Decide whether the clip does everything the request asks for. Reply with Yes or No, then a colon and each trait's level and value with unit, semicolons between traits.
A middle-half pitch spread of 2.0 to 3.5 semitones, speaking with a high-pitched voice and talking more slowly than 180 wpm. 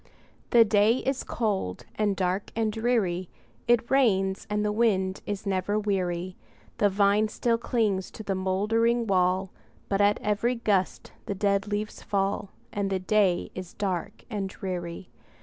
Yes: narrow, 2.4 semitones; high, 200 Hz; average, 150 wpm